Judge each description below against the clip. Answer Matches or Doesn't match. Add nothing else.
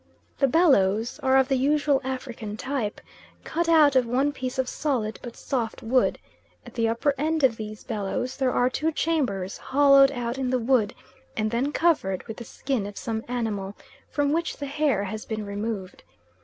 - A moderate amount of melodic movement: Matches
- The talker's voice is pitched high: Matches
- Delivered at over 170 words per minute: Matches